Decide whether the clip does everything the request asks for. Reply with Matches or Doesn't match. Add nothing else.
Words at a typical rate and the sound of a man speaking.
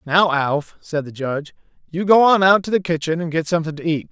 Doesn't match